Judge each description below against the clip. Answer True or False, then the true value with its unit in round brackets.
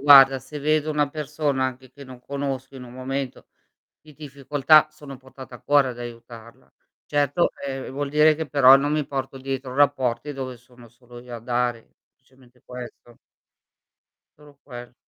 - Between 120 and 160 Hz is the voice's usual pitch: True (135 Hz)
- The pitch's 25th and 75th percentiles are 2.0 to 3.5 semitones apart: True (2.5 semitones)